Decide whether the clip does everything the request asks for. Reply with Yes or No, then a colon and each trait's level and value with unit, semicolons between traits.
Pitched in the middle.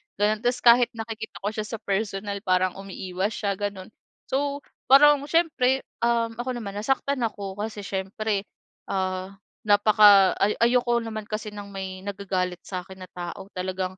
No: high, 205 Hz